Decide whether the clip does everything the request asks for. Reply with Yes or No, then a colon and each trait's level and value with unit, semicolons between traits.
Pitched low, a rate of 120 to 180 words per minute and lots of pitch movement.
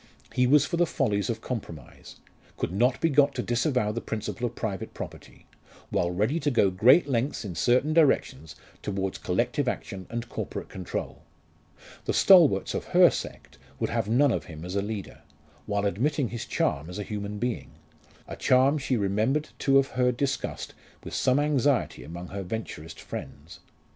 Yes: low, 115 Hz; average, 175 wpm; wide, 5.7 semitones